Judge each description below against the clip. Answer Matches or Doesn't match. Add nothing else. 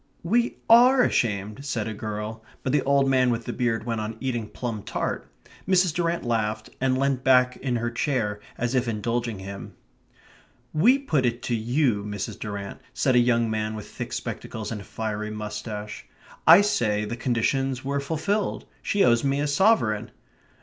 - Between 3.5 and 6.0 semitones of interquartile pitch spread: Matches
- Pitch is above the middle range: Doesn't match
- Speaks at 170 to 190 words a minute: Matches